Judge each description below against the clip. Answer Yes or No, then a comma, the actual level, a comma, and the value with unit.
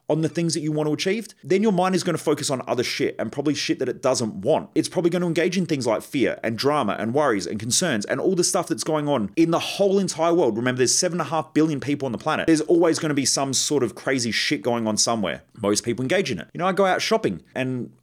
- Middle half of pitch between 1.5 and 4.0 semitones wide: No, average, 4.5 semitones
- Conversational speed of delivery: No, fast, 285 wpm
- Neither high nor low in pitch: Yes, medium, 155 Hz